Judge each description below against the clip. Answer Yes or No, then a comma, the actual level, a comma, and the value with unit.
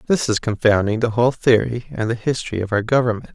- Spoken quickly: Yes, fast, 215 wpm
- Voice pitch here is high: No, low, 115 Hz